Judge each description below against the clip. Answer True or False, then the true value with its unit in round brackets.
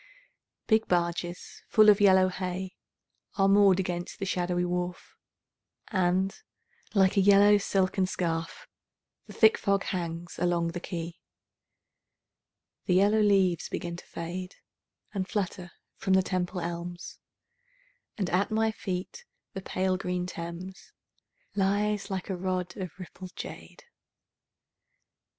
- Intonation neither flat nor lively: False (1.9 semitones)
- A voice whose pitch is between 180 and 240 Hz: True (185 Hz)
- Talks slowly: True (125 wpm)